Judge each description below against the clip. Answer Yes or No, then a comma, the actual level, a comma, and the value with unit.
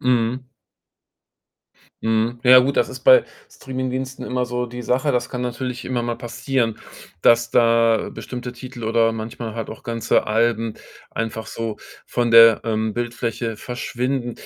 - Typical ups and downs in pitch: No, narrow, 1.7 semitones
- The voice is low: Yes, low, 120 Hz